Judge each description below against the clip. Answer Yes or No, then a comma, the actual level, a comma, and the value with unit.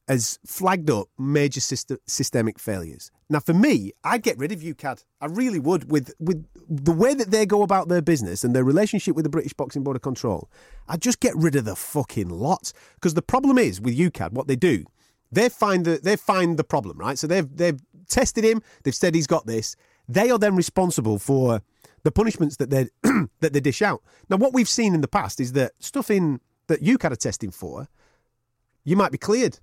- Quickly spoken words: Yes, fast, 215 wpm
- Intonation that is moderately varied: No, wide, 6.4 semitones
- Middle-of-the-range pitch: Yes, medium, 155 Hz